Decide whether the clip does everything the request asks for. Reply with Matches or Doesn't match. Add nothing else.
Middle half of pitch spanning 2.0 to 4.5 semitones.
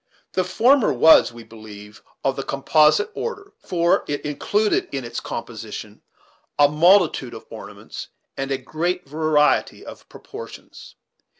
Doesn't match